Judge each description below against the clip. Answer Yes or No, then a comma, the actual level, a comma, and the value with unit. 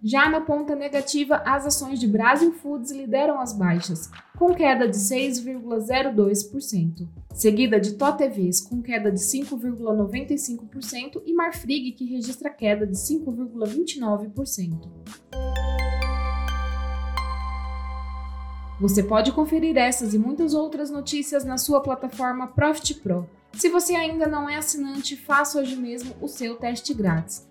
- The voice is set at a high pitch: Yes, very high, 250 Hz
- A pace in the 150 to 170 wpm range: No, average, 125 wpm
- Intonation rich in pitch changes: Yes, wide, 5.9 semitones